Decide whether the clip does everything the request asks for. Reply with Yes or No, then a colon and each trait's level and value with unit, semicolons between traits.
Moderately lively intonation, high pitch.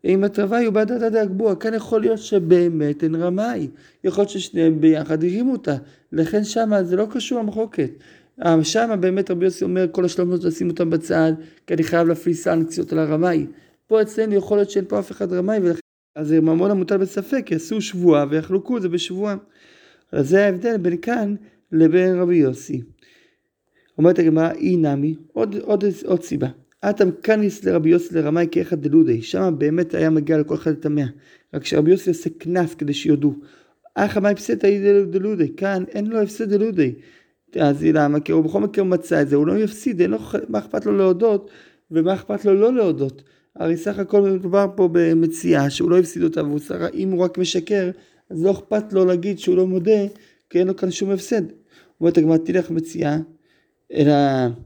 No: average, 4.0 semitones; medium, 180 Hz